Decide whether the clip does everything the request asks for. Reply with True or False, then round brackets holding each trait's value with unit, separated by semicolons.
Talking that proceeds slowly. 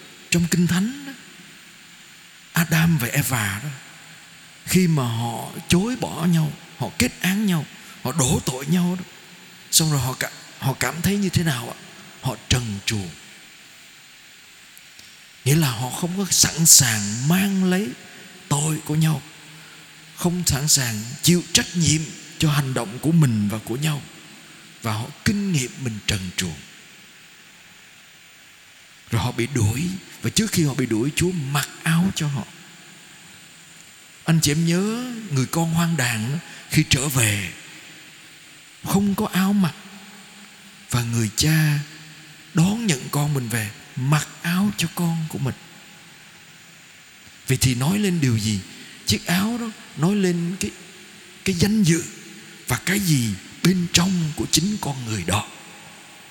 True (145 wpm)